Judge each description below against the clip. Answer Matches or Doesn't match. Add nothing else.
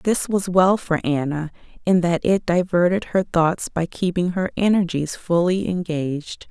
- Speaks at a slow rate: Doesn't match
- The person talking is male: Doesn't match